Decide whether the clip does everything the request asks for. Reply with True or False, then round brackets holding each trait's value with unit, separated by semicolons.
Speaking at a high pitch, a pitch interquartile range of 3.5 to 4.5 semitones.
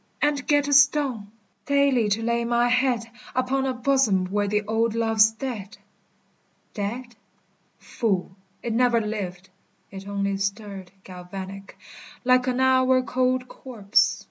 True (230 Hz; 4.2 semitones)